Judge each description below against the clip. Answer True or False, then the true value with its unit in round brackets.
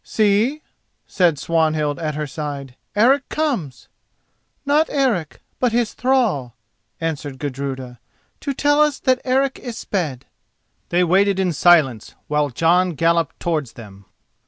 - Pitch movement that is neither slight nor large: False (8.9 semitones)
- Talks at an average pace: False (130 wpm)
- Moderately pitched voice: True (170 Hz)